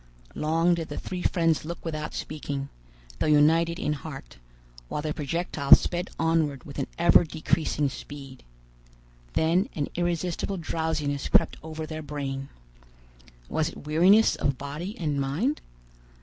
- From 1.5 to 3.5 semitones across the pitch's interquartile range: Yes, average, 2.7 semitones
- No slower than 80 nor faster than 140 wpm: Yes, slow, 135 wpm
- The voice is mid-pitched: Yes, medium, 155 Hz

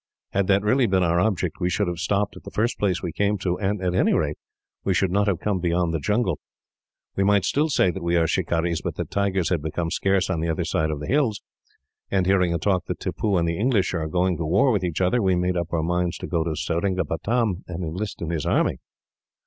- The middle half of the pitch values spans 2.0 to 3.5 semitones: Yes, average, 2.9 semitones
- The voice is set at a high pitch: No, very low, 90 Hz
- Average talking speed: No, fast, 245 wpm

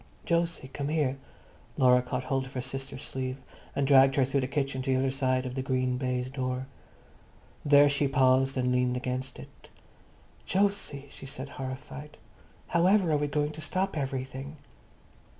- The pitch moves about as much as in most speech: No, narrow, 2.0 semitones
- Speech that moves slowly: No, average, 170 wpm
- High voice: No, low, 135 Hz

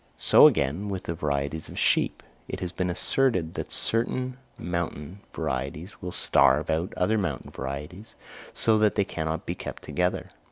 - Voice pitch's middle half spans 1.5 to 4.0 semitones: No, average, 4.4 semitones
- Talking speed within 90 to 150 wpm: No, average, 160 wpm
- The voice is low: Yes, very low, 90 Hz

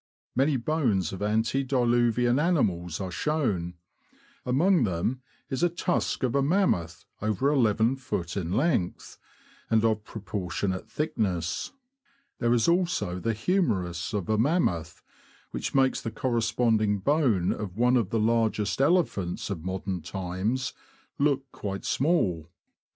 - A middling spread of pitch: No, wide, 6.3 semitones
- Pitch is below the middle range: Yes, low, 110 Hz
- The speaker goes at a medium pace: No, slow, 130 wpm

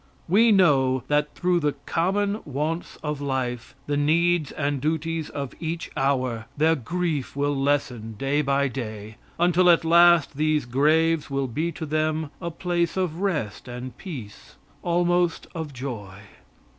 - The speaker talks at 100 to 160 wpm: Yes, average, 145 wpm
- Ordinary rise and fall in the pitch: Yes, average, 4.1 semitones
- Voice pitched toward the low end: No, medium, 150 Hz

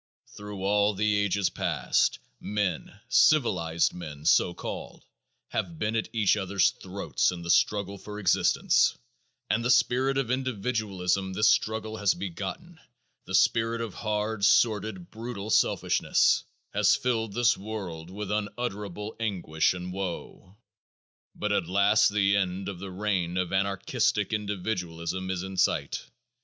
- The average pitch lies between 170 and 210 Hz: No, low, 100 Hz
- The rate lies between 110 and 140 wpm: Yes, slow, 135 wpm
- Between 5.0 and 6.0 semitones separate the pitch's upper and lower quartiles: No, average, 2.8 semitones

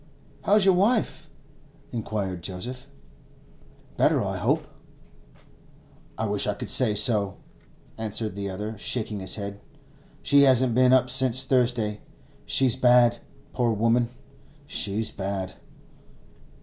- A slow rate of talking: Yes, slow, 115 wpm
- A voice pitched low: Yes, low, 115 Hz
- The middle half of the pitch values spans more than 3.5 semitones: Yes, average, 3.9 semitones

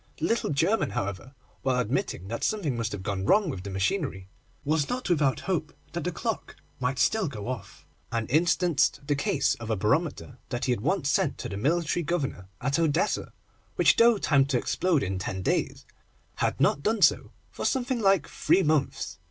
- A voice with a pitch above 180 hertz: No, medium, 140 Hz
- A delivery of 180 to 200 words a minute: Yes, average, 190 wpm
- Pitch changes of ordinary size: No, wide, 7.1 semitones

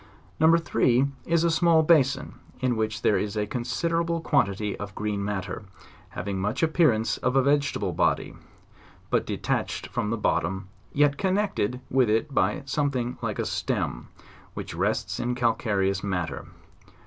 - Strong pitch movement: Yes, wide, 6.2 semitones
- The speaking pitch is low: Yes, low, 125 Hz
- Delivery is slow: No, average, 150 wpm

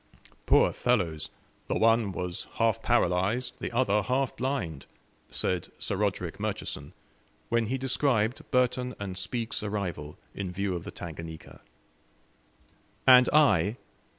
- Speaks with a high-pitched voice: No, low, 105 Hz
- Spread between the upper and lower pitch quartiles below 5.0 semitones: No, wide, 5.6 semitones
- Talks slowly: Yes, slow, 125 wpm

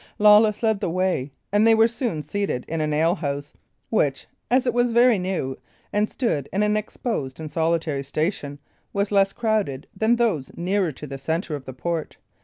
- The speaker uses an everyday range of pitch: No, wide, 6.3 semitones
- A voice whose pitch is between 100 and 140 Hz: No, medium, 185 Hz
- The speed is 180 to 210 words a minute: Yes, average, 185 wpm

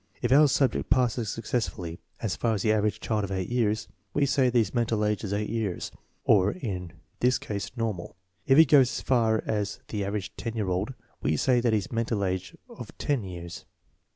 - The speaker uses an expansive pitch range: No, average, 3.5 semitones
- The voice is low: Yes, low, 110 Hz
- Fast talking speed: Yes, fast, 210 wpm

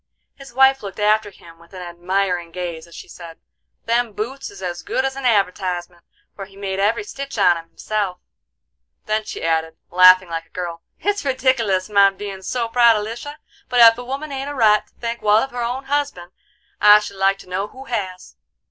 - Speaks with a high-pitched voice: Yes, high, 210 Hz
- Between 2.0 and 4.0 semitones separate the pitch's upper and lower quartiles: No, average, 5.0 semitones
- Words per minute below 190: No, fast, 205 wpm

